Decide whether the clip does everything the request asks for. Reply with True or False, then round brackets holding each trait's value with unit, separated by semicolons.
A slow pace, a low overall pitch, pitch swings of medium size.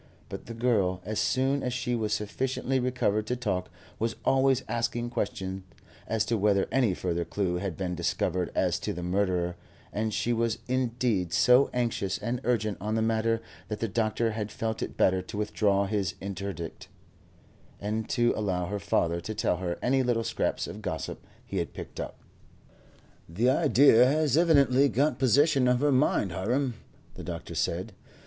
False (170 wpm; 110 Hz; 4.3 semitones)